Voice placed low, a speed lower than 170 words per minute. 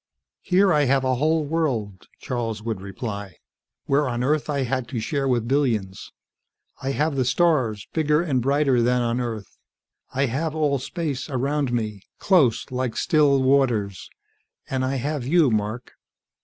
Yes: low, 130 Hz; average, 155 wpm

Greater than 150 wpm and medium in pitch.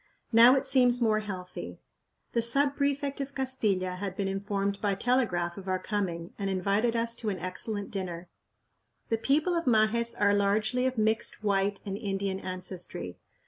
No: average, 165 wpm; high, 205 Hz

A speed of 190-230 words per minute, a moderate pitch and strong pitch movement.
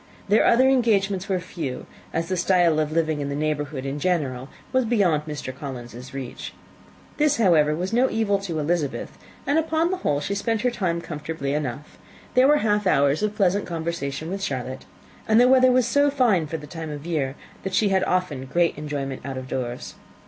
Yes: average, 195 wpm; medium, 170 Hz; wide, 6.3 semitones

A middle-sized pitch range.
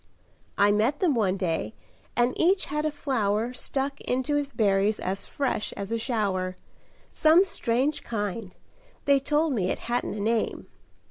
No: wide, 5.8 semitones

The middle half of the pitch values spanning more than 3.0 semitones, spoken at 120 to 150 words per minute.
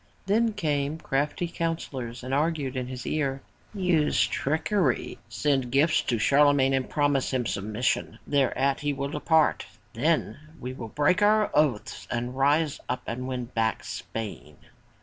Yes: average, 3.5 semitones; average, 140 wpm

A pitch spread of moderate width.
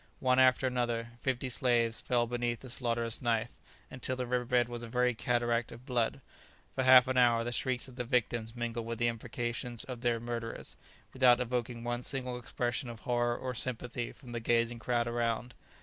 No: narrow, 1.1 semitones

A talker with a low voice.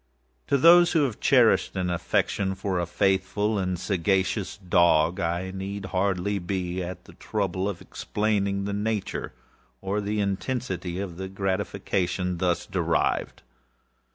Yes: very low, 95 Hz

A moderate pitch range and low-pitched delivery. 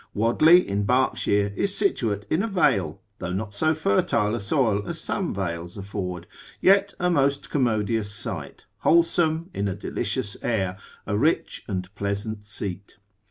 No: wide, 7.2 semitones; low, 105 Hz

